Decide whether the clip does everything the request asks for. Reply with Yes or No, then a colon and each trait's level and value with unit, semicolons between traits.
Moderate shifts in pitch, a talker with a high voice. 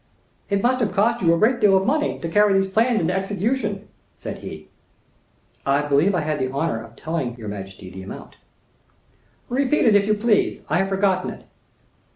No: wide, 6.3 semitones; high, 195 Hz